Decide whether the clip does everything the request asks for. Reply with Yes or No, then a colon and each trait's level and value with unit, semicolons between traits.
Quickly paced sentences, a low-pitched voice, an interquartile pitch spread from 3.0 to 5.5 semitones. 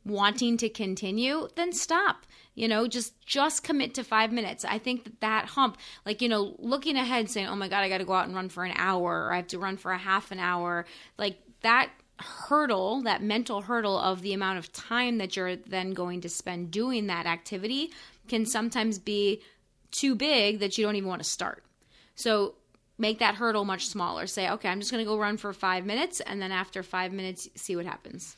No: fast, 220 wpm; high, 205 Hz; average, 3.7 semitones